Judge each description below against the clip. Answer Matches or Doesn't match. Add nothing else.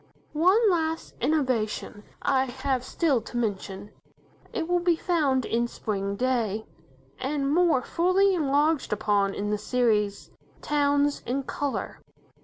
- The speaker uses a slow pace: Matches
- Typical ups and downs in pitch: Doesn't match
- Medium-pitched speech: Doesn't match